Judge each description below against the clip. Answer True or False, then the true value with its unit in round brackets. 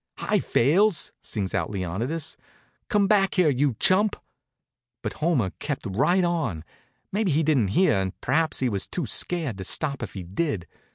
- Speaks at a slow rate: False (165 wpm)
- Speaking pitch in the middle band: True (145 Hz)